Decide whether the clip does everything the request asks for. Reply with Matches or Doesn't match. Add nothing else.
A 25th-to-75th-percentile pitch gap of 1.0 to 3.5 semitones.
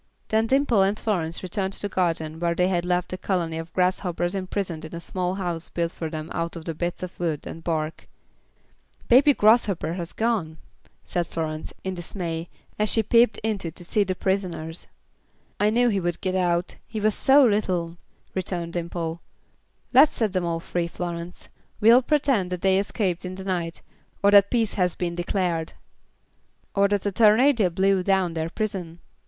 Matches